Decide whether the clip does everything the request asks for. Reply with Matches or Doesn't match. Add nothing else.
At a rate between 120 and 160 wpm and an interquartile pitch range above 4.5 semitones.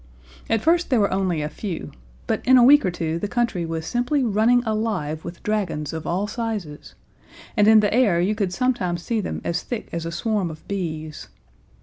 Doesn't match